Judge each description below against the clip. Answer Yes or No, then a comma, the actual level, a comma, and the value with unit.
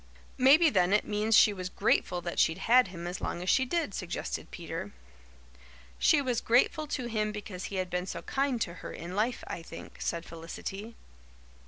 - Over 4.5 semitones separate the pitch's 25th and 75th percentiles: Yes, wide, 5.4 semitones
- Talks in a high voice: Yes, high, 205 Hz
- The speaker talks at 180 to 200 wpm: Yes, average, 190 wpm